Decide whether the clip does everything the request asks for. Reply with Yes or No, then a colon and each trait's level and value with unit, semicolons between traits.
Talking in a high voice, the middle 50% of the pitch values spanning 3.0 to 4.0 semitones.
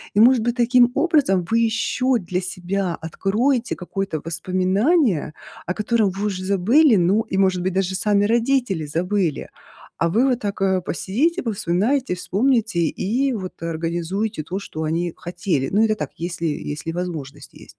No: high, 195 Hz; average, 4.7 semitones